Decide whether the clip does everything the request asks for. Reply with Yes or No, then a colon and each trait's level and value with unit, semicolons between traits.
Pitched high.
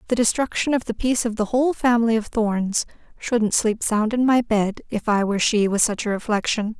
Yes: high, 225 Hz